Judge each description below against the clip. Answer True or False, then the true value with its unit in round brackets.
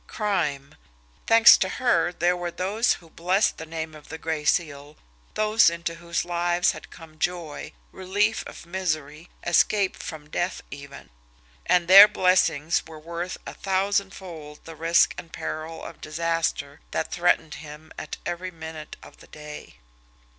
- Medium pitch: True (170 Hz)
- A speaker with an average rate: True (150 wpm)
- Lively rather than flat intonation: False (2.8 semitones)